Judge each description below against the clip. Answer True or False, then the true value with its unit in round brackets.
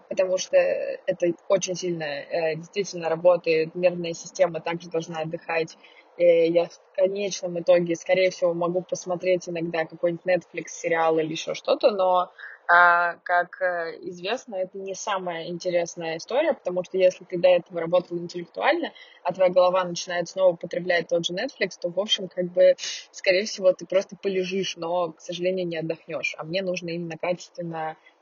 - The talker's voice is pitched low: False (180 Hz)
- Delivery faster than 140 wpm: True (155 wpm)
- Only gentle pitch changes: True (1.5 semitones)